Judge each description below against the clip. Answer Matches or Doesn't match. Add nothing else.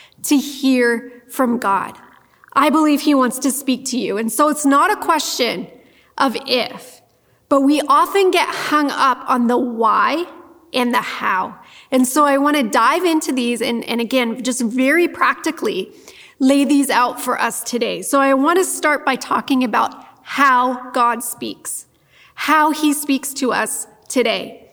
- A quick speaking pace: Doesn't match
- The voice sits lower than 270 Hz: Doesn't match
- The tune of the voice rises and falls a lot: Doesn't match